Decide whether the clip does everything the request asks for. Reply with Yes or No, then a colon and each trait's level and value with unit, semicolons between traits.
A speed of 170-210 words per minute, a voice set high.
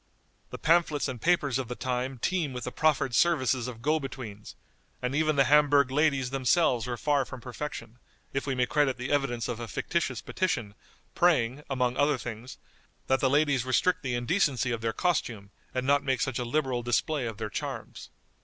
No: average, 190 wpm; low, 130 Hz